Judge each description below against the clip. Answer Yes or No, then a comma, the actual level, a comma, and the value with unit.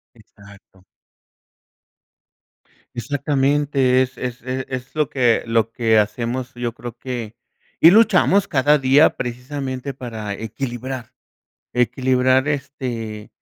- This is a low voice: Yes, low, 130 Hz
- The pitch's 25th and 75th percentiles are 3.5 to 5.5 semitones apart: No, average, 2.7 semitones